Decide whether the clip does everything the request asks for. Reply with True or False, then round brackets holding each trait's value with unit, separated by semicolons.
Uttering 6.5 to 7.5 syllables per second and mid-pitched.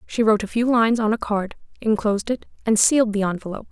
False (7.0 syllables/s; 215 Hz)